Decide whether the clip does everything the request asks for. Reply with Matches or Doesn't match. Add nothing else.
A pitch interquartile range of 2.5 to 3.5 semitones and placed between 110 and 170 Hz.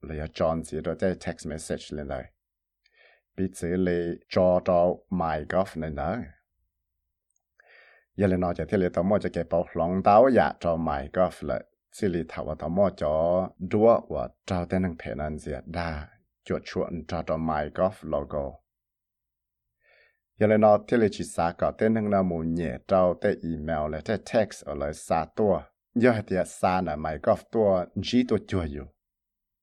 Doesn't match